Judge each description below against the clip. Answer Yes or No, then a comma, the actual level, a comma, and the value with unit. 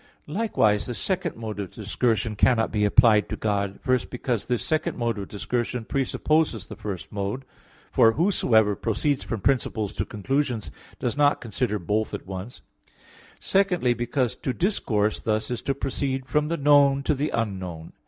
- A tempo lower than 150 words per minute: No, average, 165 wpm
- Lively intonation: No, average, 4.7 semitones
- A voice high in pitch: No, low, 120 Hz